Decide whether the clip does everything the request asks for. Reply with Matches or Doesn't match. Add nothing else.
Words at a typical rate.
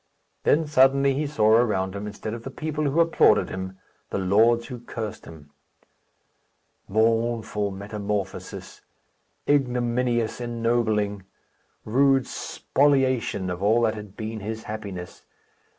Doesn't match